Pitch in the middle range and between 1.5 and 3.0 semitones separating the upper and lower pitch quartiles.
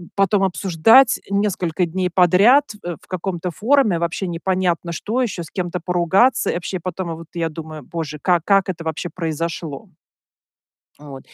Yes: medium, 175 Hz; average, 2.7 semitones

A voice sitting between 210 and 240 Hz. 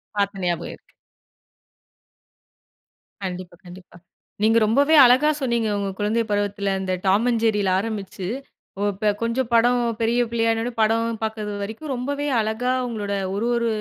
Yes: high, 220 Hz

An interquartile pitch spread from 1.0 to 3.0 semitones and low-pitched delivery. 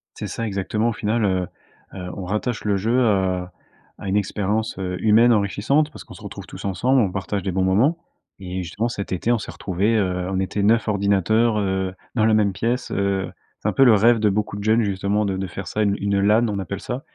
Yes: narrow, 2.6 semitones; low, 100 Hz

